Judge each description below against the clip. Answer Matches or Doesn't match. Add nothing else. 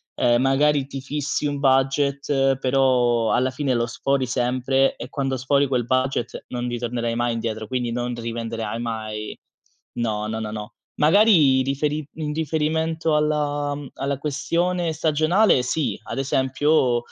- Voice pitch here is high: Doesn't match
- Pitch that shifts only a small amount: Doesn't match